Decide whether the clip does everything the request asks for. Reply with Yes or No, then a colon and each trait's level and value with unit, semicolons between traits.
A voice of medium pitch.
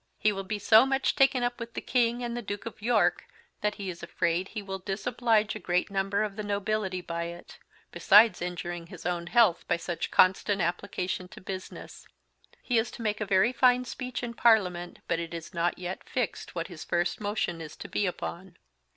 No: high, 195 Hz